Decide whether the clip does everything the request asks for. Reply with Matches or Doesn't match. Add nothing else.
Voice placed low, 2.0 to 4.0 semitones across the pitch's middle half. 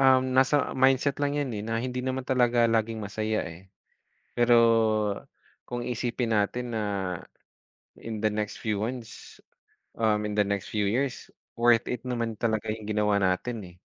Matches